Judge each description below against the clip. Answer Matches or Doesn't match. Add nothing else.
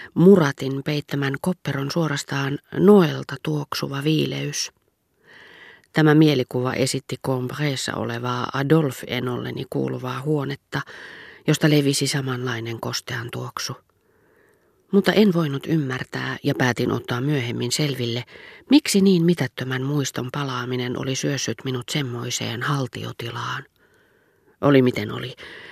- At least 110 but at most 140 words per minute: Doesn't match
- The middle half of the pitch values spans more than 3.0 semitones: Matches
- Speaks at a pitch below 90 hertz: Doesn't match